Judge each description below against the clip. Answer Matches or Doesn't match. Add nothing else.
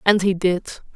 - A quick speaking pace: Doesn't match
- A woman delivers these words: Matches